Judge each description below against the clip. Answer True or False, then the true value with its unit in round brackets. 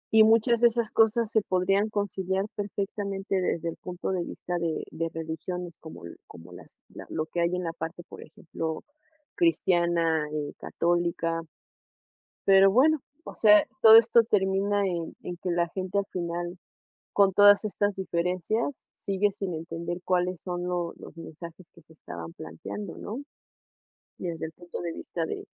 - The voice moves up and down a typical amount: True (3.2 semitones)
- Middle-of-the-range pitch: True (180 Hz)